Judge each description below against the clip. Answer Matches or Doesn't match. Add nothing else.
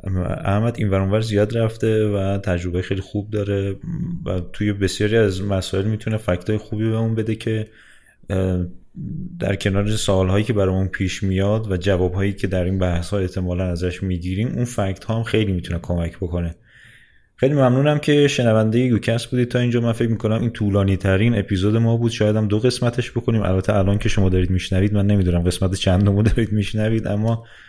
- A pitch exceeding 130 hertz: Doesn't match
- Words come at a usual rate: Doesn't match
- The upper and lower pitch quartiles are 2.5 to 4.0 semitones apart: Matches